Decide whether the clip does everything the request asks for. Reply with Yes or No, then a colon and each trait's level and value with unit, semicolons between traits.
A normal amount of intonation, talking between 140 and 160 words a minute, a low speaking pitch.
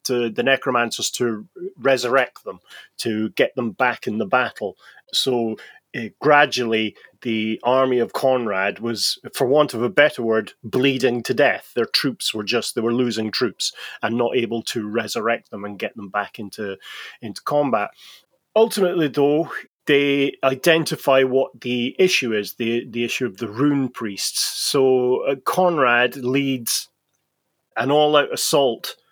Yes: average, 3.3 semitones; average, 150 wpm; low, 125 Hz